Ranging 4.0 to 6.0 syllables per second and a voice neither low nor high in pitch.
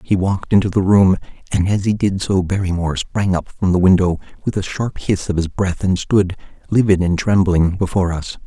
No: 5.5 syllables/s; very low, 95 Hz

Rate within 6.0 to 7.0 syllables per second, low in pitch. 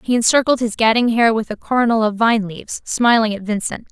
No: 6.1 syllables/s; high, 225 Hz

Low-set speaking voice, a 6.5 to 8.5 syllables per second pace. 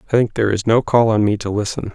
Yes: low, 110 Hz; 6.6 syllables/s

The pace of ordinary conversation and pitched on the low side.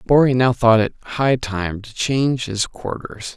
Yes: average, 180 wpm; low, 120 Hz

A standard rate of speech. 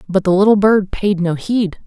No: fast, 225 wpm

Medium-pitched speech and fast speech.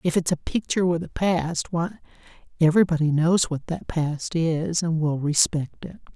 No: medium, 165 Hz; average, 175 wpm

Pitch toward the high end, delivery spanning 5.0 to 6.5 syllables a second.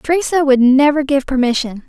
Yes: very high, 275 Hz; 5.5 syllables/s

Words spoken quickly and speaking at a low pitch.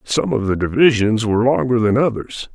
No: average, 190 wpm; low, 115 Hz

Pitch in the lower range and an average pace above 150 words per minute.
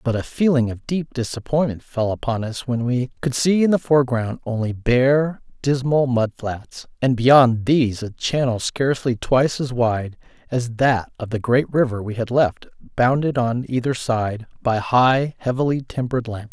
Yes: low, 125 Hz; average, 175 wpm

